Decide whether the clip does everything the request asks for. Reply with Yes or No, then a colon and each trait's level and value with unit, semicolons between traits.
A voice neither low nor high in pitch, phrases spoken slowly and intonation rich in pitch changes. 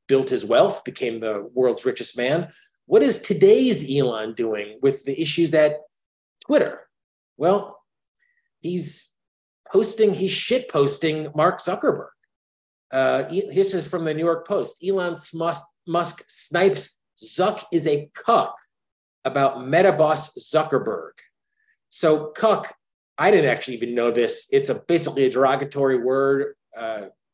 Yes: medium, 165 Hz; slow, 130 wpm; wide, 6.2 semitones